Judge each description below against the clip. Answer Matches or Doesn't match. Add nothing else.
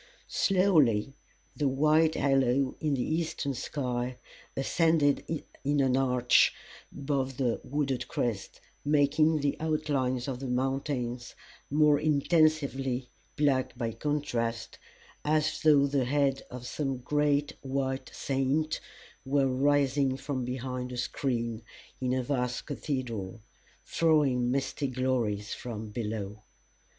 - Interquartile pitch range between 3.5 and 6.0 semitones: Doesn't match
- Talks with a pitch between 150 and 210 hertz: Doesn't match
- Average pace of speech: Doesn't match